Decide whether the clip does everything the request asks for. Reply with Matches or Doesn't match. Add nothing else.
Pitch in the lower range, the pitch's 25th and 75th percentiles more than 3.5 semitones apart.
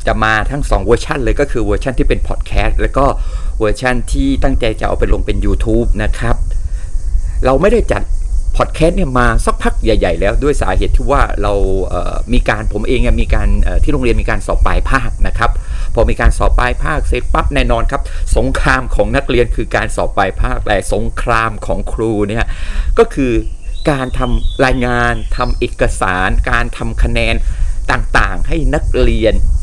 Matches